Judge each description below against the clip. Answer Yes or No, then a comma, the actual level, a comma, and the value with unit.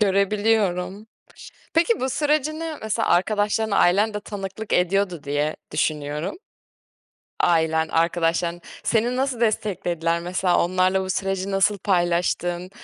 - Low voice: No, high, 190 Hz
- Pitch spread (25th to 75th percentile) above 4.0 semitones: No, average, 3.7 semitones